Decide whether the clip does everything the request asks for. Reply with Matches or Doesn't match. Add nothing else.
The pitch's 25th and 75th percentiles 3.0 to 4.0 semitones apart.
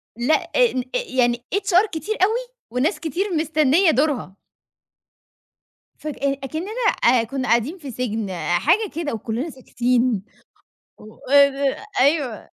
Doesn't match